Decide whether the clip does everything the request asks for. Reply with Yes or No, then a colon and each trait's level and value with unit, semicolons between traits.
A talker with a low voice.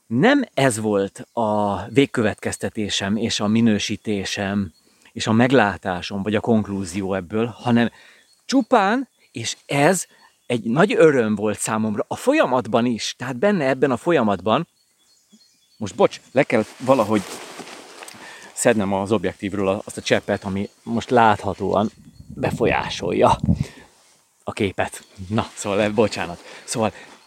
Yes: low, 110 Hz